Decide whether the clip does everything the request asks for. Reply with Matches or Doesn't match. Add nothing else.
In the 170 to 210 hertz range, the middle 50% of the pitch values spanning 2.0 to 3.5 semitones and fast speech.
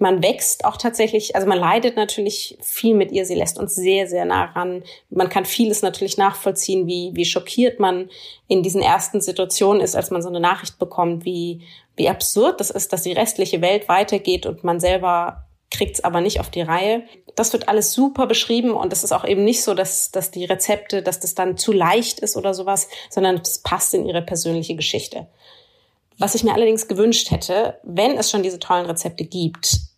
Matches